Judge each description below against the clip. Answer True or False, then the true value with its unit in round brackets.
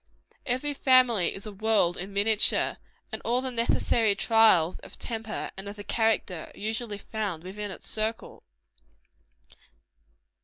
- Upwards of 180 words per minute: False (145 wpm)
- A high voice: True (215 Hz)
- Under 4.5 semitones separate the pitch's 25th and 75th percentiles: True (2.5 semitones)